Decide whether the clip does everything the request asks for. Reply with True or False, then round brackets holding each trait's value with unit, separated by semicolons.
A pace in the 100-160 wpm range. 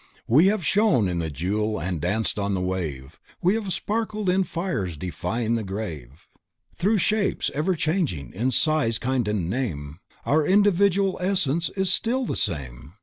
True (155 wpm)